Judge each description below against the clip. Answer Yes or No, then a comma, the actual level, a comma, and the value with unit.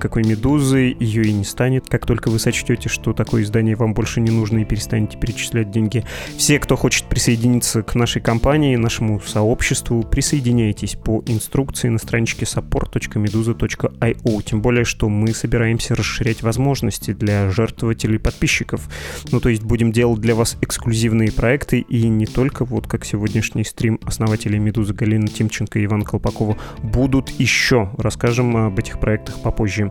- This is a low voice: Yes, low, 115 Hz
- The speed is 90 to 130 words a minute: No, average, 155 wpm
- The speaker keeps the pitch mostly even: Yes, narrow, 1.8 semitones